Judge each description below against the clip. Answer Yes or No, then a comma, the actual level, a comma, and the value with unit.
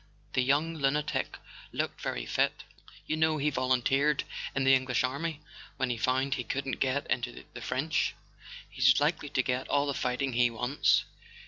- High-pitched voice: No, low, 135 Hz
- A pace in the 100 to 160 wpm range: No, average, 175 wpm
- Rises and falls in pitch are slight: Yes, narrow, 2.2 semitones